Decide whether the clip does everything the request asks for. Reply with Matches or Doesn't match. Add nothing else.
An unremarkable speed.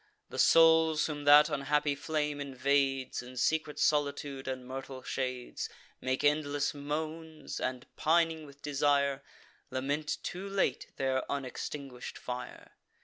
Doesn't match